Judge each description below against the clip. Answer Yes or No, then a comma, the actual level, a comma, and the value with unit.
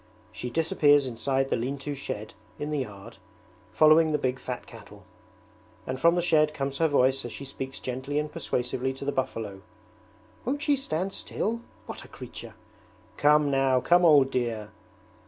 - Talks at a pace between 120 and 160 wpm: No, average, 170 wpm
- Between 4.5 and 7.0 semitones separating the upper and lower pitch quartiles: No, average, 3.1 semitones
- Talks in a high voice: No, medium, 140 Hz